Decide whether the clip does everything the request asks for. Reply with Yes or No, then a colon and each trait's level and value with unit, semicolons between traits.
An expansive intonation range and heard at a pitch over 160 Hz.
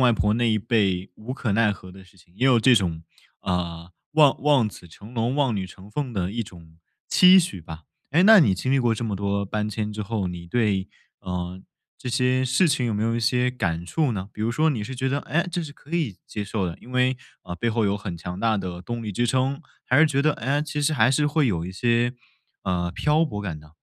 No: wide, 5.7 semitones; low, 115 Hz